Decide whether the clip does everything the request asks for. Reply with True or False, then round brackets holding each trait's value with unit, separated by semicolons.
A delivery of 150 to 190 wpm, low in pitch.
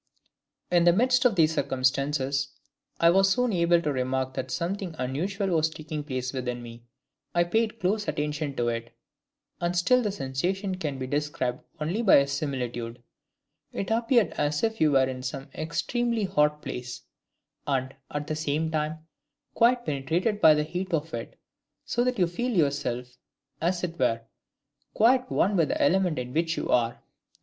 False (165 wpm; 155 Hz)